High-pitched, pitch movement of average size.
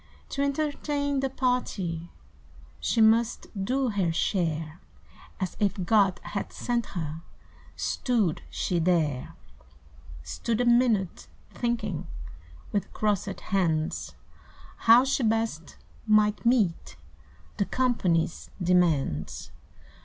No: high, 205 Hz; wide, 5.9 semitones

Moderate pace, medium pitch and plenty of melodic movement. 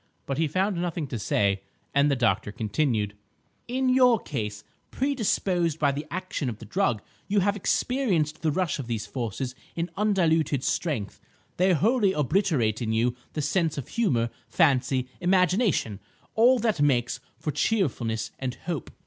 Yes: average, 150 wpm; medium, 150 Hz; wide, 7.8 semitones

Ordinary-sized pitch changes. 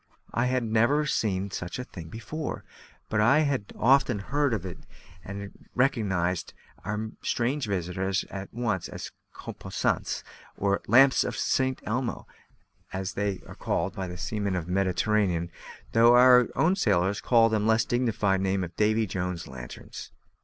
Yes: average, 4.2 semitones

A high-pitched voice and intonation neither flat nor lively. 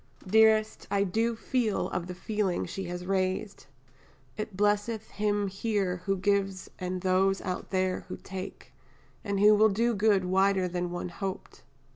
No: high, 195 Hz; narrow, 2.2 semitones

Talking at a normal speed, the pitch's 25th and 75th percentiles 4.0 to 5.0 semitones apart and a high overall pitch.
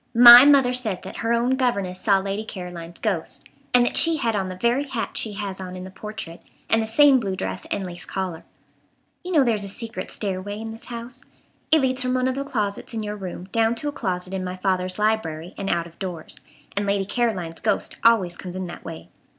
No: fast, 225 wpm; average, 4.4 semitones; high, 210 Hz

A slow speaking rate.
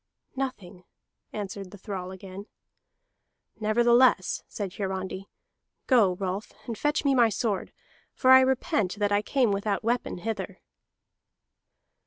Yes: slow, 120 wpm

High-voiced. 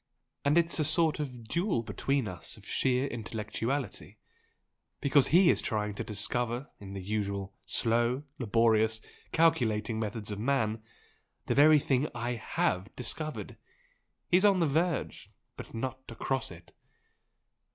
No: low, 120 Hz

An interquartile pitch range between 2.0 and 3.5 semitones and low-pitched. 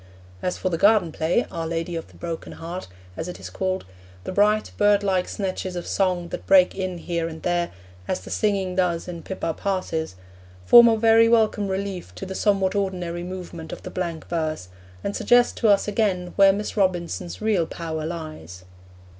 No: average, 2.9 semitones; medium, 185 Hz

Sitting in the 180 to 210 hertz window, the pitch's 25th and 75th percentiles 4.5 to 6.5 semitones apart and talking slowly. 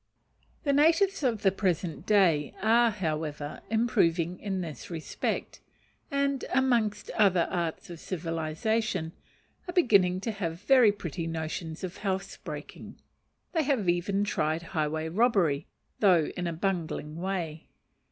Yes: medium, 185 Hz; average, 5.0 semitones; slow, 125 wpm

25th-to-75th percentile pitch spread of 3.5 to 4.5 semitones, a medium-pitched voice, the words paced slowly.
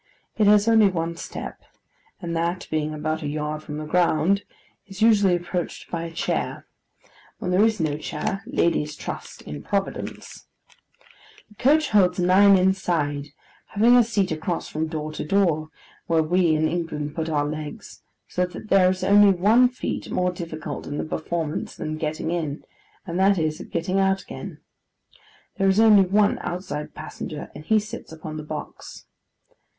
No: average, 4.1 semitones; medium, 175 Hz; average, 165 wpm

